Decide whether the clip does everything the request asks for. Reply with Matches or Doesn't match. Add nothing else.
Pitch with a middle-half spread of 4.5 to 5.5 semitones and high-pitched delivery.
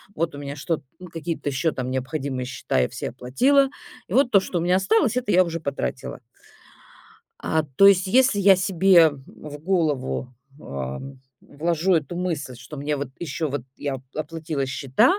Doesn't match